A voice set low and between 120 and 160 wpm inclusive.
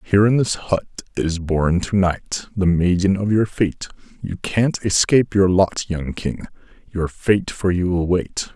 No: very low, 95 Hz; average, 180 wpm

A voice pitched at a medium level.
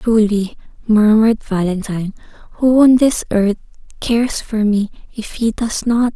No: high, 220 Hz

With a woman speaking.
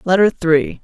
Yes: female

